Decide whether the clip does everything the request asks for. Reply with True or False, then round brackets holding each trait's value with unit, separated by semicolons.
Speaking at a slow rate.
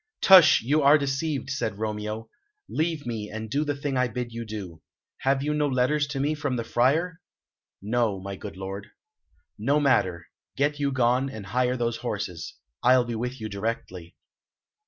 False (175 wpm)